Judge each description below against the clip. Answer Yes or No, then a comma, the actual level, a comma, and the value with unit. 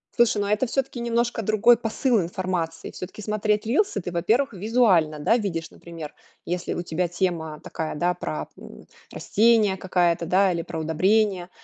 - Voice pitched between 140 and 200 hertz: Yes, high, 190 Hz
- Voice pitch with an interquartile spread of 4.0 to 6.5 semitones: Yes, average, 4.6 semitones